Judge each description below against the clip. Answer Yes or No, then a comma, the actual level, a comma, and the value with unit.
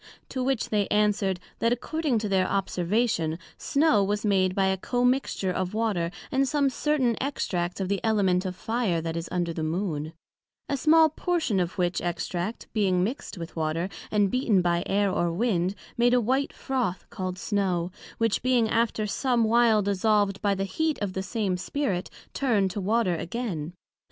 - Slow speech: No, average, 175 wpm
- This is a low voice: No, high, 200 Hz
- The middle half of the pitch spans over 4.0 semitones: Yes, average, 4.7 semitones